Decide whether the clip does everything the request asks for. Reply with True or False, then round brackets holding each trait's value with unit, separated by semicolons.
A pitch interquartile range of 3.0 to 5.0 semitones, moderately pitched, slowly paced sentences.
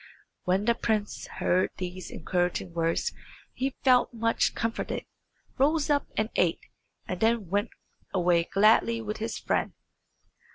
False (4.3 semitones; 215 Hz; 130 wpm)